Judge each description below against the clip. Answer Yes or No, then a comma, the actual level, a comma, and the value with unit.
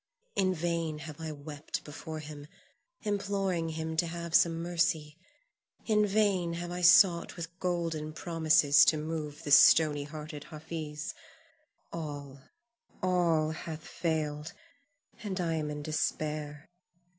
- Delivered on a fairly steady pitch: Yes, narrow, 2.2 semitones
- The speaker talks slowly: Yes, slow, 125 wpm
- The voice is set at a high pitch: No, medium, 160 Hz